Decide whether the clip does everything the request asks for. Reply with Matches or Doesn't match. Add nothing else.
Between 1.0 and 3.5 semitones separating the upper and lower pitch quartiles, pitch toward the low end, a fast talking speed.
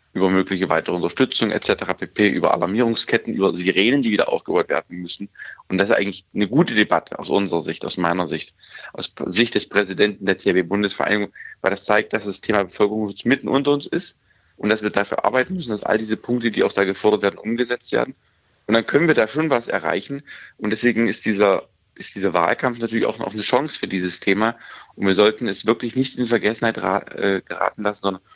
Matches